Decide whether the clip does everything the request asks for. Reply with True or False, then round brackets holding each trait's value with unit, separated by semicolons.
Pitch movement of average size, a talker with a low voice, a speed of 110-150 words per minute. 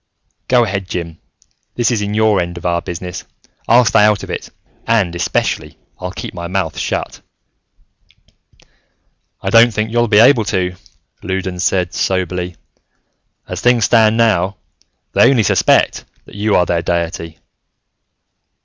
True (4.0 semitones; 95 Hz; 140 wpm)